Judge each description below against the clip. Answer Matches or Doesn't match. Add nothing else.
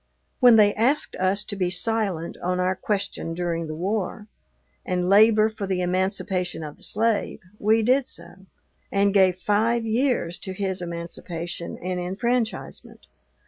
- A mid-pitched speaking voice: Doesn't match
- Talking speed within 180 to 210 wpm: Doesn't match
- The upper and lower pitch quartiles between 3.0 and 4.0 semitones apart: Matches